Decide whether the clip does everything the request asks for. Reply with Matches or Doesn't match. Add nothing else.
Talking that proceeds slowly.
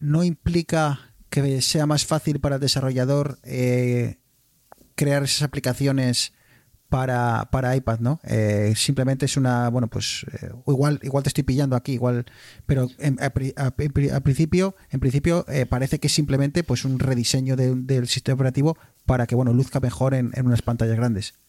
Doesn't match